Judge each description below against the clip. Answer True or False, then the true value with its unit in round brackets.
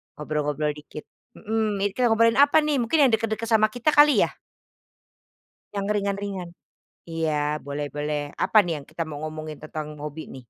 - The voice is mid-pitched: True (165 Hz)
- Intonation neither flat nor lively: False (6.7 semitones)